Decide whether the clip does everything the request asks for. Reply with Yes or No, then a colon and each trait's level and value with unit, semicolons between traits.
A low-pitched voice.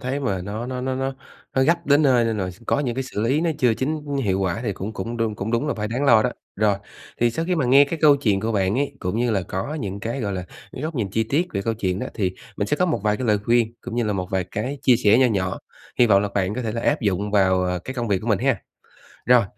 Yes: low, 115 Hz